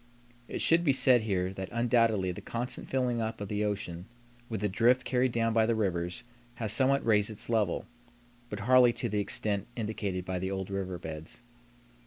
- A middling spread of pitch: Yes, average, 3.6 semitones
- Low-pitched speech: Yes, low, 110 Hz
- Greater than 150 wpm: Yes, average, 190 wpm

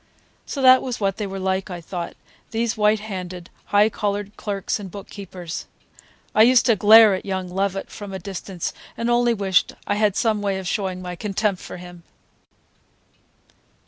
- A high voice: Yes, high, 200 Hz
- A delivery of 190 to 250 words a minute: No, average, 175 wpm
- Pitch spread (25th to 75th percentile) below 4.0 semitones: Yes, narrow, 2.4 semitones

